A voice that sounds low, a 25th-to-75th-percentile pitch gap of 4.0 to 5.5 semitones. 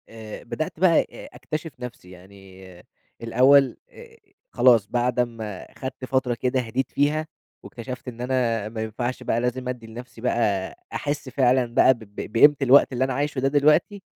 No: low, 125 Hz; average, 2.9 semitones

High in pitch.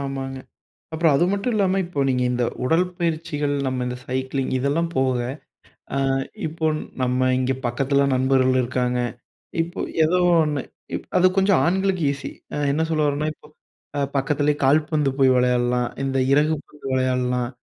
No: medium, 140 Hz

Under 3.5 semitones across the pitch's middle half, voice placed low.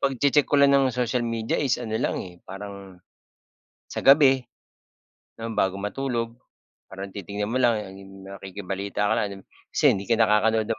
No: average, 4.0 semitones; low, 110 Hz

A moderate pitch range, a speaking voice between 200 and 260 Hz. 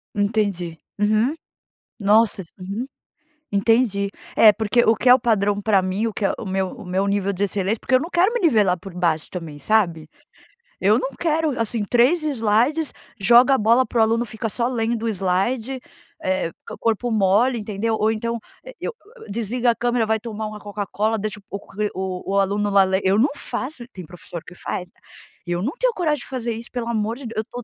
Yes: average, 3.4 semitones; high, 215 Hz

